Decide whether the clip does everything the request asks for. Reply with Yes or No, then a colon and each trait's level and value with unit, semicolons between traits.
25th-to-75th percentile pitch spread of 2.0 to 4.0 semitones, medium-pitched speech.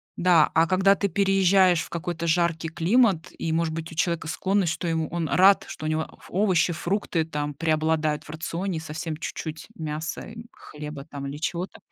Yes: narrow, 2.6 semitones; medium, 165 Hz